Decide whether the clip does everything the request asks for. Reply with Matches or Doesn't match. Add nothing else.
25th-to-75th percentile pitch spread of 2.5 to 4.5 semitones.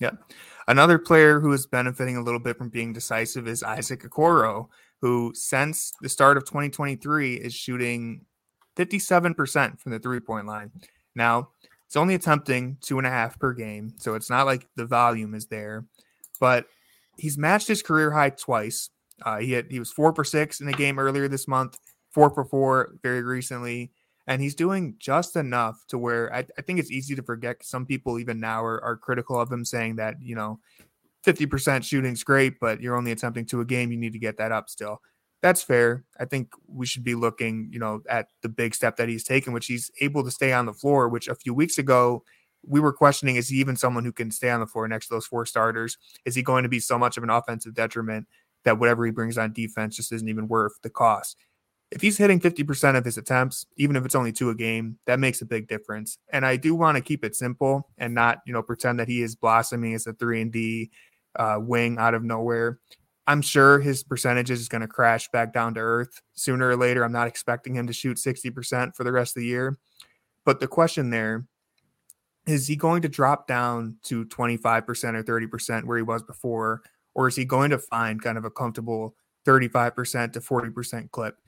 Matches